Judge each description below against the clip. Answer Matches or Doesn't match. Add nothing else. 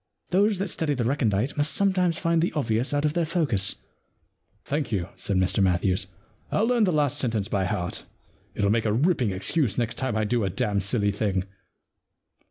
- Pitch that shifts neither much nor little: Doesn't match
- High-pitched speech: Doesn't match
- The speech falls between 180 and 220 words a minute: Matches